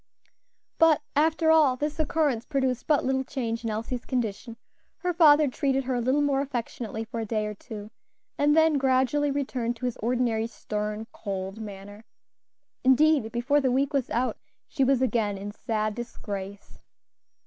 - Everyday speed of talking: Yes, average, 160 wpm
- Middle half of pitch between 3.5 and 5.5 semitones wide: Yes, average, 4.2 semitones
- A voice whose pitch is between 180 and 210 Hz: No, very high, 250 Hz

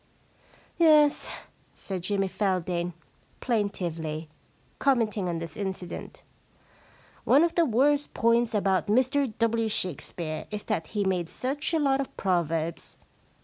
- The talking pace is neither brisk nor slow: No, slow, 130 wpm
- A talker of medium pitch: No, high, 205 Hz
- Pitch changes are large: Yes, wide, 6.7 semitones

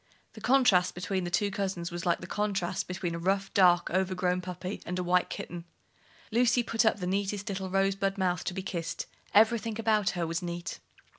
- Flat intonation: Yes, narrow, 2.3 semitones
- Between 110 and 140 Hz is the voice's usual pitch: No, high, 190 Hz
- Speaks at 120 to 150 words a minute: No, average, 195 wpm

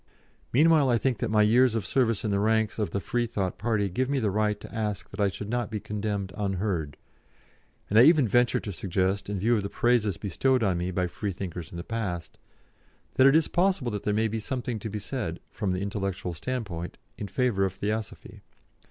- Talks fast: Yes, fast, 215 wpm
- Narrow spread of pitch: No, average, 3.6 semitones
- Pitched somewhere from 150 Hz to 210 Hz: No, low, 105 Hz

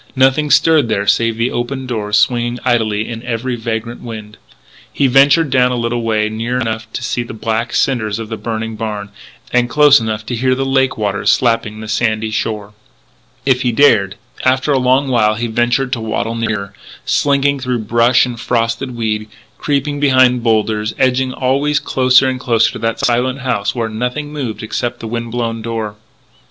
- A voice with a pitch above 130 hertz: No, low, 120 Hz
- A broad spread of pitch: No, average, 2.7 semitones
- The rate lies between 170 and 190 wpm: Yes, average, 185 wpm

